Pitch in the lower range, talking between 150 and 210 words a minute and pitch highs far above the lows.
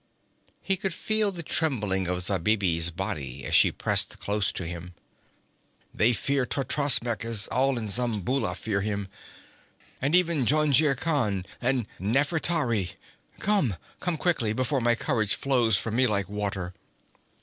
No: low, 115 Hz; slow, 135 wpm; wide, 6.0 semitones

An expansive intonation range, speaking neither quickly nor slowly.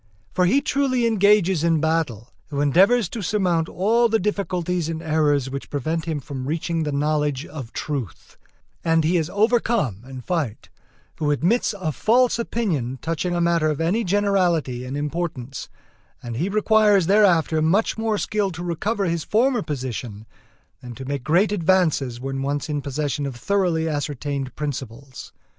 Yes: wide, 5.7 semitones; average, 160 wpm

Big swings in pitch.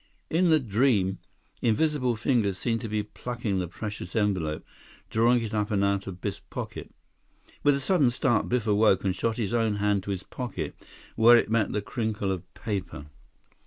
No: average, 3.3 semitones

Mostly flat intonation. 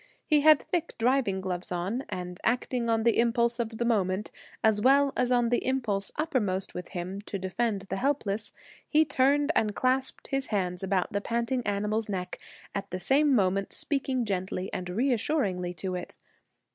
No: average, 5.2 semitones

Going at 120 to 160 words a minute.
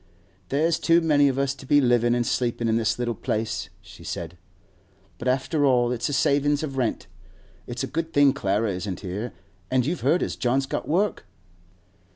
No: average, 190 wpm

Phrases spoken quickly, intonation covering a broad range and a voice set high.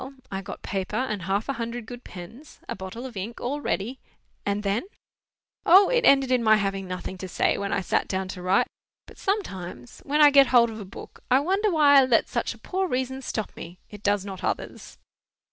Yes: fast, 215 wpm; wide, 5.7 semitones; high, 225 Hz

